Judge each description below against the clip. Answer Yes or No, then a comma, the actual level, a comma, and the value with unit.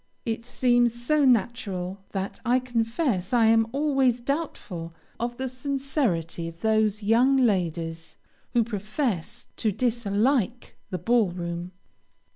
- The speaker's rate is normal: No, slow, 120 wpm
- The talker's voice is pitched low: No, high, 230 Hz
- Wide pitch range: No, average, 4.8 semitones